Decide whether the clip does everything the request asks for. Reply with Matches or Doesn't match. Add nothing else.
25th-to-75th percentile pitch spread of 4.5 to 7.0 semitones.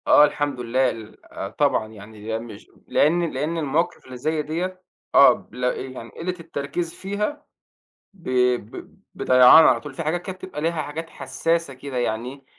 Matches